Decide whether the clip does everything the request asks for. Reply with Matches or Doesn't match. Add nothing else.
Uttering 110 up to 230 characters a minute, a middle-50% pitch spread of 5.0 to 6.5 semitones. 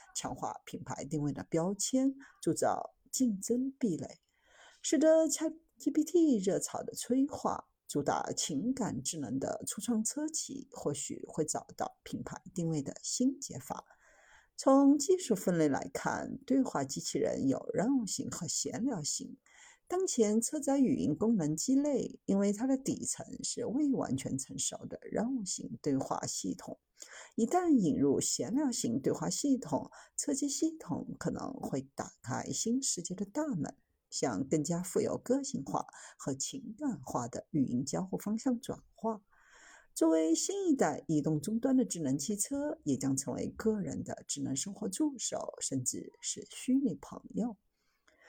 Matches